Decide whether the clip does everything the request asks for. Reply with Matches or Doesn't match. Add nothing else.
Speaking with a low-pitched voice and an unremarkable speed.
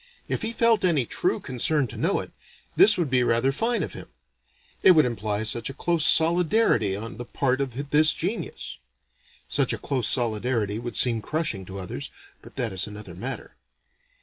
Matches